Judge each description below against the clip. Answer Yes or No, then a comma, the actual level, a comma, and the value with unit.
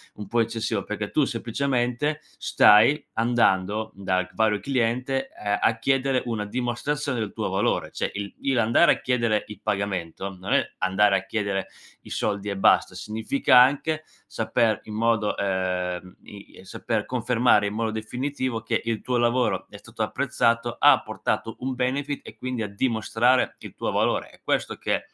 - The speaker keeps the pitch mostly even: No, average, 3.5 semitones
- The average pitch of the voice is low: Yes, low, 115 Hz